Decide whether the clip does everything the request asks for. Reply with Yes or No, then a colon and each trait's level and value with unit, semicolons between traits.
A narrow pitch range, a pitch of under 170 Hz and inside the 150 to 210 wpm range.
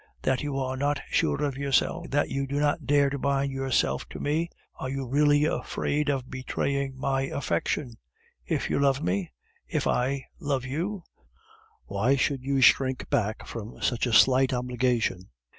Yes: narrow, 2.0 semitones; low, 135 Hz; average, 165 wpm